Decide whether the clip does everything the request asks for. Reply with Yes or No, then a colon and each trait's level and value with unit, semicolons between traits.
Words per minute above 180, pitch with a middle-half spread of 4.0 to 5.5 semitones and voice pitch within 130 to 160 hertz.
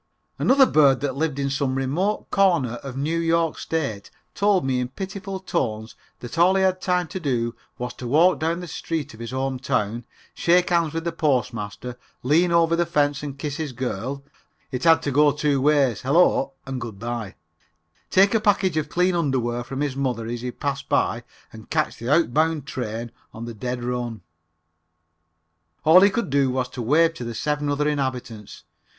Yes: average, 190 wpm; average, 5.0 semitones; medium, 140 Hz